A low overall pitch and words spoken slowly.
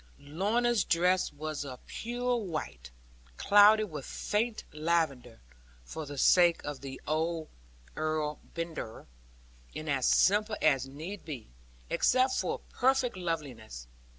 No: medium, 160 Hz; slow, 120 wpm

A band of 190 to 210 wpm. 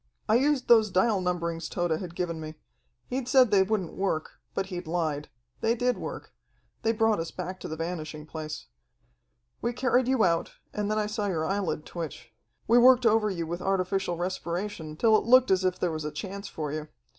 Yes: average, 200 wpm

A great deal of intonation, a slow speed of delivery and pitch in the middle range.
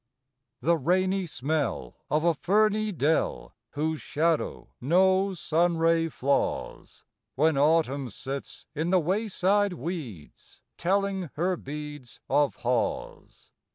No: average, 4.3 semitones; slow, 105 wpm; medium, 165 Hz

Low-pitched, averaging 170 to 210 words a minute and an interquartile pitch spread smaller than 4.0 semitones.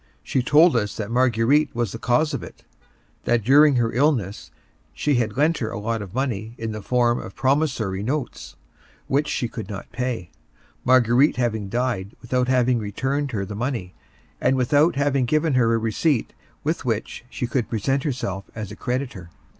Yes: low, 120 Hz; average, 180 wpm; average, 3.5 semitones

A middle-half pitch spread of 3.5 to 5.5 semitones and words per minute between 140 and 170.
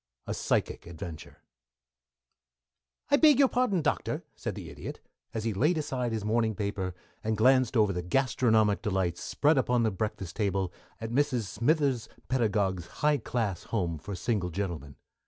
Yes: average, 5.2 semitones; average, 155 wpm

